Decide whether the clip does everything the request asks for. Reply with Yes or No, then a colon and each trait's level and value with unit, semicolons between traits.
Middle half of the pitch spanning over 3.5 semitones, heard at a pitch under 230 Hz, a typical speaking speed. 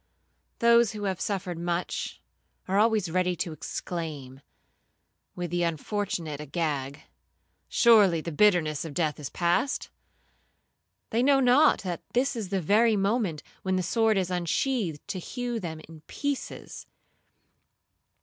No: average, 5.2 semitones; medium, 185 Hz; slow, 130 wpm